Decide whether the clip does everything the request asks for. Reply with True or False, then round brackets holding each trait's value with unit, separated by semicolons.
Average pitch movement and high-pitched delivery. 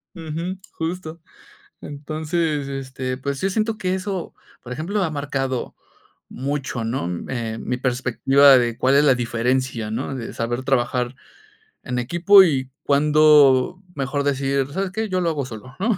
False (4.2 semitones; 140 Hz)